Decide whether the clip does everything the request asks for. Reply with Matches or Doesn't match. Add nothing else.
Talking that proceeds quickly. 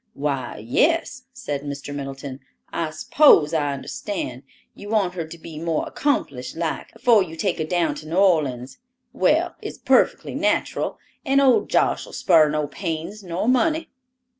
Doesn't match